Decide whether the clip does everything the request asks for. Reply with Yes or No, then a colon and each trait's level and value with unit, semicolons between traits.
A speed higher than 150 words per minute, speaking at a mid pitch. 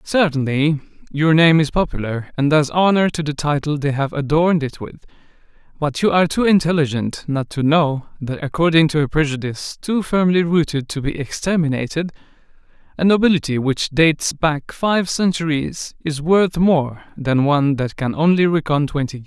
Yes: average, 165 wpm; medium, 155 Hz